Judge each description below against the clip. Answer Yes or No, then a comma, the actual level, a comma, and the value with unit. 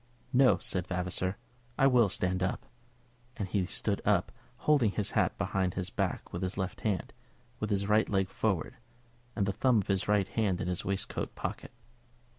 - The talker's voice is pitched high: No, very low, 95 Hz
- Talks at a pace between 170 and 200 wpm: Yes, average, 180 wpm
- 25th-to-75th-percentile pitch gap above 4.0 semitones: No, average, 2.7 semitones